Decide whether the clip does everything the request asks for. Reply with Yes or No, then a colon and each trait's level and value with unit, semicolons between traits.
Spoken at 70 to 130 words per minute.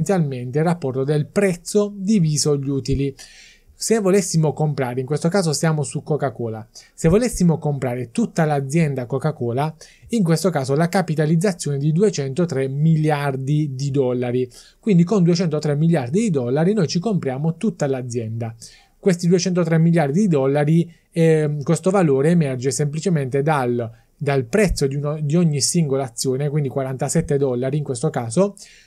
No: average, 145 wpm